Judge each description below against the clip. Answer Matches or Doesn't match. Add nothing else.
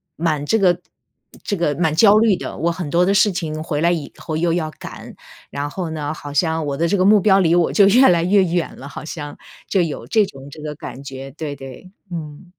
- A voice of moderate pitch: Matches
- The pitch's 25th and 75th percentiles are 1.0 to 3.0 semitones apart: Doesn't match